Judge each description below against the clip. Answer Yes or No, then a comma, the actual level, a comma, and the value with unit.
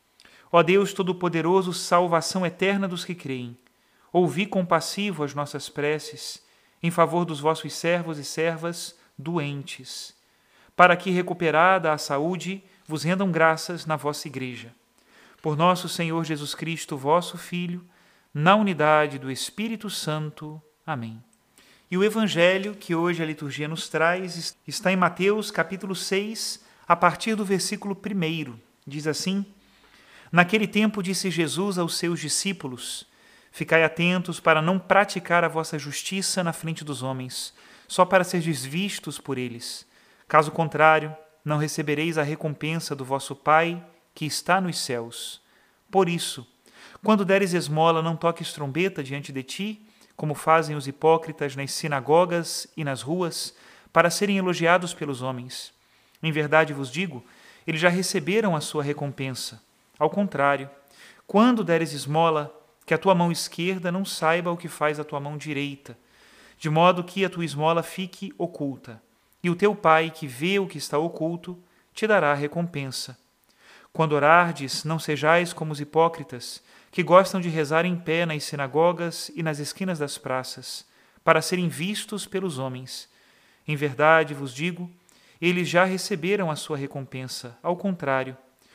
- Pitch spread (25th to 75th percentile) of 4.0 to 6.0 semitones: No, average, 3.3 semitones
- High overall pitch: No, medium, 165 Hz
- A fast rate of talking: No, average, 145 wpm